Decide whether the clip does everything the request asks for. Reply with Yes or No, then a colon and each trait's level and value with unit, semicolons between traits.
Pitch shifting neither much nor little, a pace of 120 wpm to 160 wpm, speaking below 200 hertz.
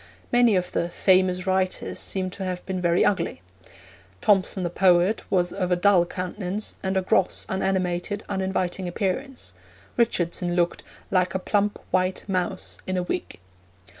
No: narrow, 1.4 semitones; average, 150 wpm; medium, 185 Hz